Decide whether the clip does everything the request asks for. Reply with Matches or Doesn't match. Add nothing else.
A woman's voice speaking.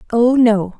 Matches